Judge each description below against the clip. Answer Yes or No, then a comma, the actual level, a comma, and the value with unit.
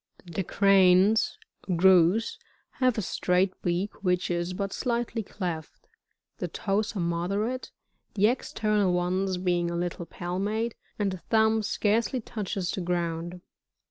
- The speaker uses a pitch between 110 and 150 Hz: No, high, 190 Hz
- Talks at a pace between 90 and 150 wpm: Yes, average, 140 wpm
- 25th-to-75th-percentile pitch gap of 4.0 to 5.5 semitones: No, average, 3.3 semitones